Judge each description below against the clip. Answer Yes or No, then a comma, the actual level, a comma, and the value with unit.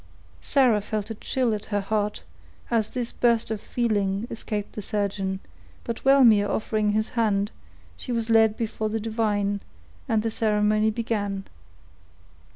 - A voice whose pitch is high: Yes, high, 215 Hz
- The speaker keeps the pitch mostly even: Yes, narrow, 1.7 semitones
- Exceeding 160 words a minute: No, average, 145 wpm